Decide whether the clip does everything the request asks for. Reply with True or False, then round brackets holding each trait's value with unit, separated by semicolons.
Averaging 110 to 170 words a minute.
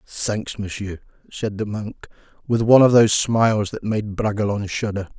True (160 wpm)